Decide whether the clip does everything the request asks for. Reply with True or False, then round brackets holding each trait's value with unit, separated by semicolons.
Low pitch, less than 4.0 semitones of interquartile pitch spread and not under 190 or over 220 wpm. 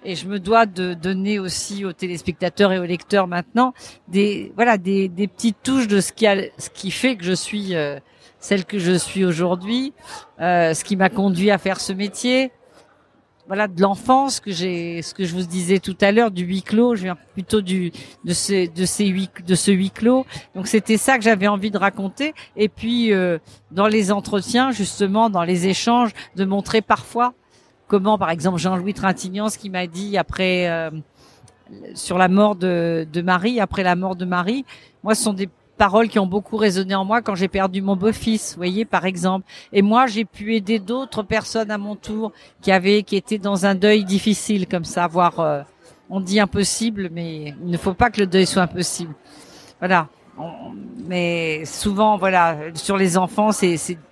False (195 Hz; 2.8 semitones; 200 wpm)